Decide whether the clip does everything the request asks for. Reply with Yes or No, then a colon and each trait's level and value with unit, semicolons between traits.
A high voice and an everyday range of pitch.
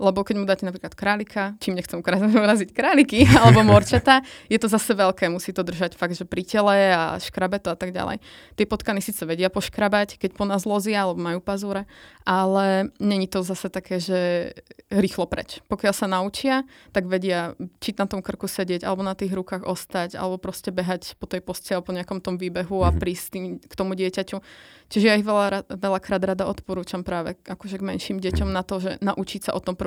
No: high, 195 Hz; narrow, 1.8 semitones